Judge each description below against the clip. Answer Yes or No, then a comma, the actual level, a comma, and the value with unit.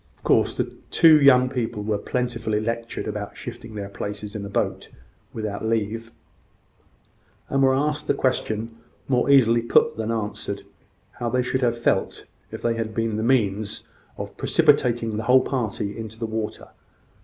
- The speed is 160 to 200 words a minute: Yes, average, 165 wpm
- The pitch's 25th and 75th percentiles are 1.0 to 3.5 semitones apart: Yes, narrow, 2.6 semitones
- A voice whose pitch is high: No, low, 115 Hz